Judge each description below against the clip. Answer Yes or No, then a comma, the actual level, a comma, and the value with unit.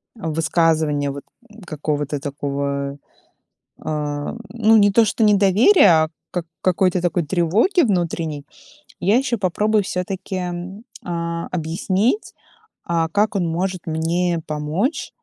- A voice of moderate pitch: Yes, medium, 170 Hz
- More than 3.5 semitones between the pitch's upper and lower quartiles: Yes, average, 4.4 semitones